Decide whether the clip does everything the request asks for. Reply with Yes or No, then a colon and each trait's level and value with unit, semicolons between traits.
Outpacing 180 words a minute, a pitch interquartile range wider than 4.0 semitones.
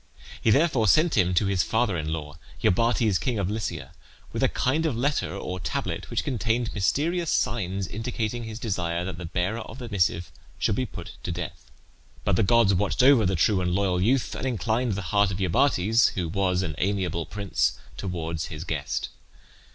Yes: average, 190 wpm; average, 4.7 semitones